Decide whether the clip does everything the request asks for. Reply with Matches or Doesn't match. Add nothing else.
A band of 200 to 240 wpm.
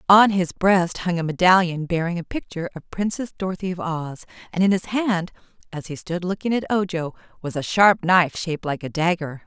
Matches